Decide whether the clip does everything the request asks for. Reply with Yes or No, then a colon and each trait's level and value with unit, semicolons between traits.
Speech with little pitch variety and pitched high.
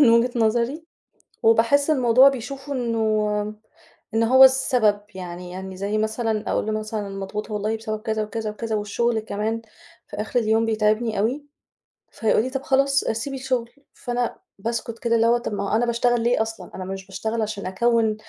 Yes: narrow, 2.2 semitones; high, 225 Hz